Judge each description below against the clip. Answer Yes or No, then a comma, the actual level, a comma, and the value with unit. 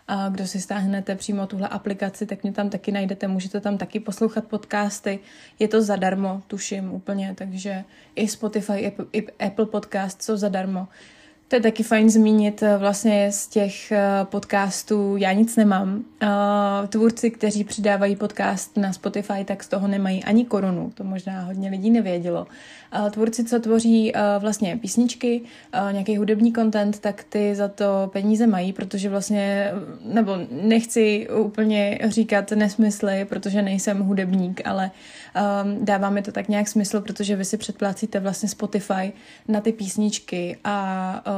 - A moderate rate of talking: Yes, average, 145 wpm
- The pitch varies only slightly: Yes, narrow, 1.6 semitones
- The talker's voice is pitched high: Yes, high, 205 Hz